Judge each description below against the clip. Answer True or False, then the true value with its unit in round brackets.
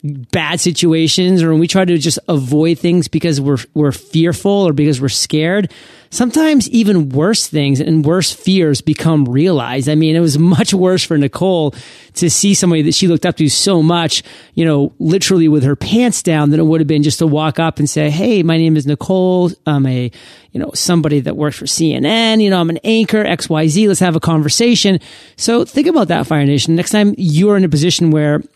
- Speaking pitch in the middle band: True (165 Hz)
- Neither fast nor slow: False (210 wpm)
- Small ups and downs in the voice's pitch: False (3.5 semitones)